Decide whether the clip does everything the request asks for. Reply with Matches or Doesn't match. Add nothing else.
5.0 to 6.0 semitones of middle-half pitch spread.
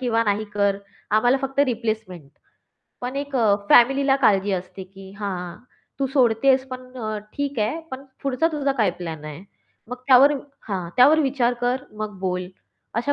Matches